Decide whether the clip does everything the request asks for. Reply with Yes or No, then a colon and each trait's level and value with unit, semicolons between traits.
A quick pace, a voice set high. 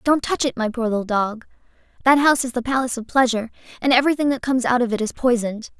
Yes: fast, 230 wpm; high, 245 Hz